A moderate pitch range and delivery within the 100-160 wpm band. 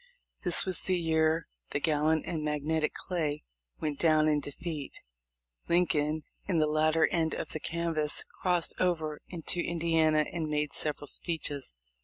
No: narrow, 1.9 semitones; average, 145 wpm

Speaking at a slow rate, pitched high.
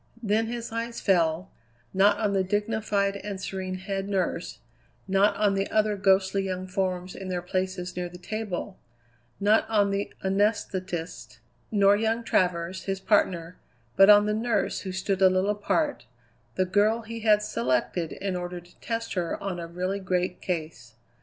No: average, 165 wpm; high, 195 Hz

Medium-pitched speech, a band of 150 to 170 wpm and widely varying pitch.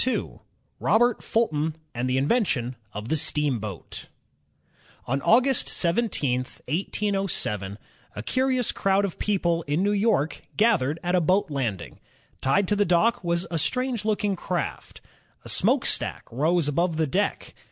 No: medium, 170 Hz; average, 140 wpm; wide, 7.0 semitones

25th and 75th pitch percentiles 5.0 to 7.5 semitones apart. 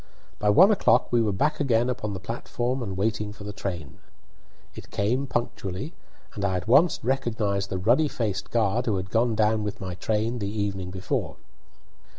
No: average, 3.5 semitones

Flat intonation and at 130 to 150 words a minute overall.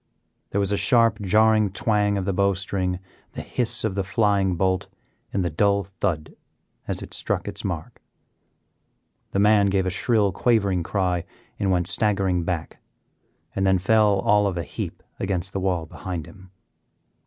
No: narrow, 1.9 semitones; average, 165 wpm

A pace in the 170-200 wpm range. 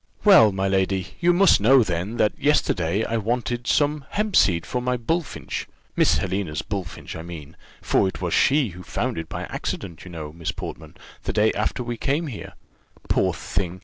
Yes: average, 180 wpm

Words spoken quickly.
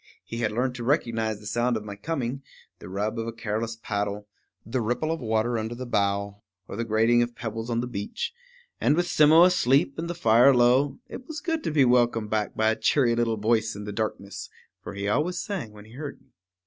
Yes: fast, 225 wpm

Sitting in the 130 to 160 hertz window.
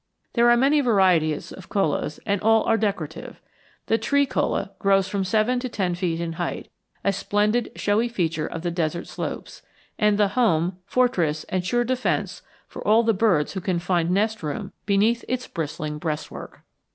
No: high, 195 Hz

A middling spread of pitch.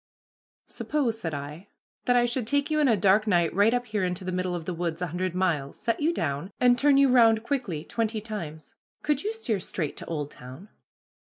No: wide, 6.3 semitones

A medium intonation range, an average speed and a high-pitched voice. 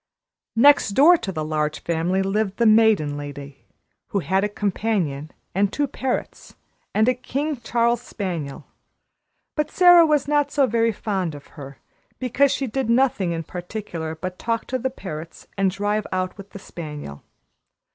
No: wide, 6.8 semitones; average, 160 wpm; high, 200 Hz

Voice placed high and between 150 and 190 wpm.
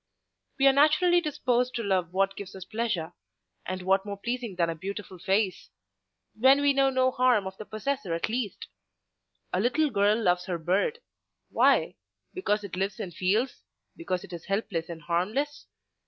Yes: high, 205 Hz; average, 165 wpm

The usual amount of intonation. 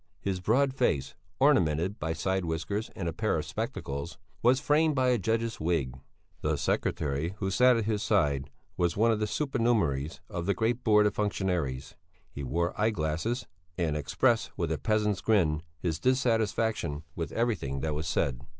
No: wide, 6.3 semitones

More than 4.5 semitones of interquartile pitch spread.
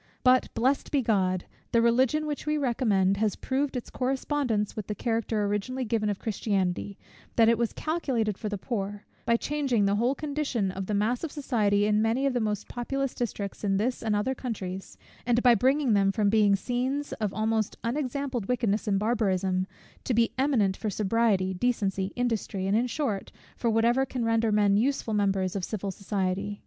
No: average, 3.9 semitones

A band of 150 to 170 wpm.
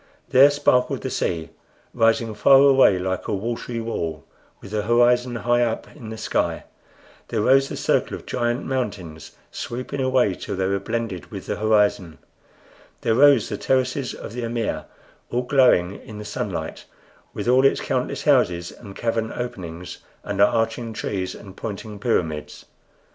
Yes: average, 160 wpm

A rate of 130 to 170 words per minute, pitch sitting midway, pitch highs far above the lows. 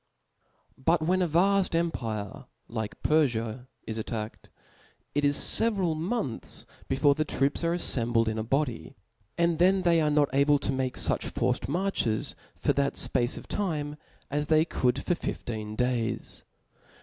Yes: average, 150 wpm; medium, 145 Hz; wide, 5.9 semitones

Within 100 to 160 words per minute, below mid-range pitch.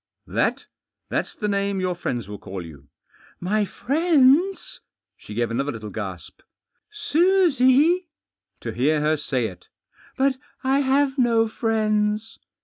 No: average, 140 wpm; high, 215 Hz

